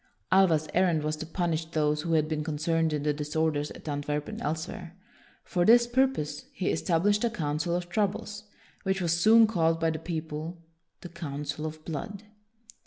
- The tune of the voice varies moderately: Yes, average, 3.1 semitones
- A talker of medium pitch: Yes, medium, 165 Hz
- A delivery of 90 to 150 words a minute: No, average, 175 wpm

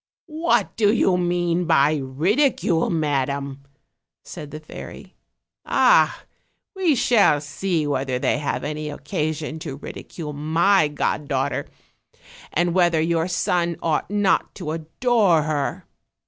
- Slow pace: Yes, slow, 120 wpm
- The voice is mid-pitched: Yes, medium, 160 Hz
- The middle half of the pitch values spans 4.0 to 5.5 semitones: No, average, 3.6 semitones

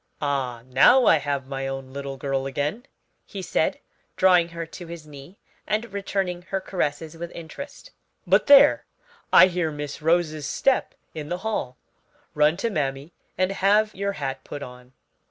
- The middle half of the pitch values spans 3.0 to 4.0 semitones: No, average, 5.3 semitones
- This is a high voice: No, medium, 160 Hz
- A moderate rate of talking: Yes, average, 160 wpm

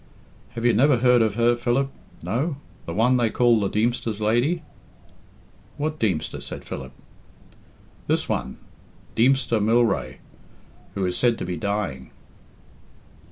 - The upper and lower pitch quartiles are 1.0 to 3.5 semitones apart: Yes, average, 3.1 semitones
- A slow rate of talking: Yes, slow, 130 wpm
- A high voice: No, low, 115 Hz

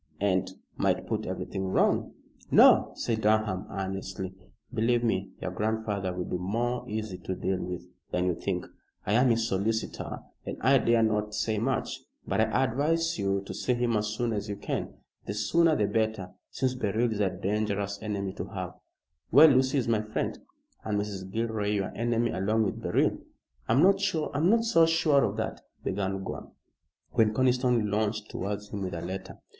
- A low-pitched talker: Yes, low, 110 Hz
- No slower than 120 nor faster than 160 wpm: No, average, 175 wpm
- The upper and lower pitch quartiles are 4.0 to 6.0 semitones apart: No, average, 3.4 semitones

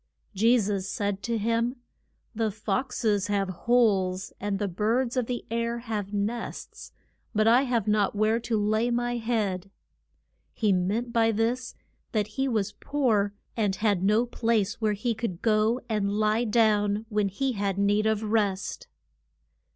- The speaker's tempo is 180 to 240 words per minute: No, average, 160 wpm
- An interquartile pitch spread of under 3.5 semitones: Yes, narrow, 2.4 semitones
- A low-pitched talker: No, high, 215 Hz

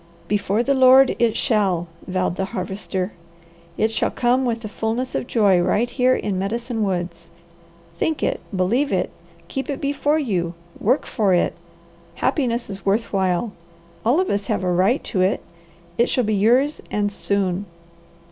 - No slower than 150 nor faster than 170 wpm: Yes, average, 165 wpm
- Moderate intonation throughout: Yes, average, 4.6 semitones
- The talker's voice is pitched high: Yes, high, 215 Hz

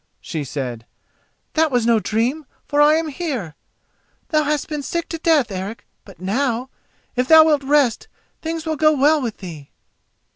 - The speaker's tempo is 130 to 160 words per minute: No, average, 170 wpm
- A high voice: Yes, very high, 275 Hz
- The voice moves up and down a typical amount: No, wide, 6.1 semitones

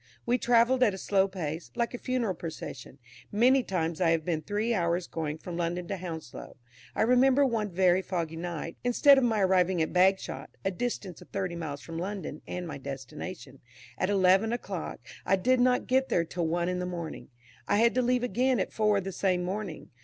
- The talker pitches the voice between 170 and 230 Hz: Yes, medium, 185 Hz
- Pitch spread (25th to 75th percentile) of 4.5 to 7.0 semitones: Yes, wide, 5.4 semitones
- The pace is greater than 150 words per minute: Yes, average, 200 wpm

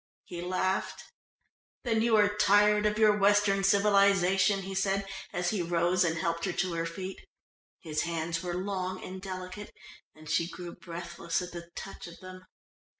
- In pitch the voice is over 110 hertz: Yes, medium, 185 Hz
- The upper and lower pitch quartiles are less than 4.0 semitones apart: Yes, narrow, 2.5 semitones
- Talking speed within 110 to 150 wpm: No, average, 165 wpm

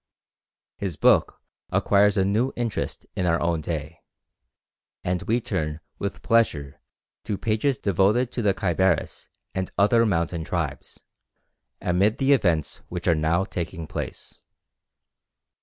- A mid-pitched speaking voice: No, very low, 95 Hz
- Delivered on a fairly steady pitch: No, average, 4.3 semitones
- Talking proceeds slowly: Yes, slow, 125 wpm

